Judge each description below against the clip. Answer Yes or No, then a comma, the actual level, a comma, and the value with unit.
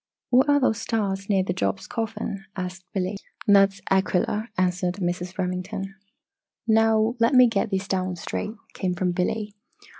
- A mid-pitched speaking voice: No, high, 195 Hz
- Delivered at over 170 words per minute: No, average, 150 wpm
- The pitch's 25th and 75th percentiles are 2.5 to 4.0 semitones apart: Yes, average, 3.0 semitones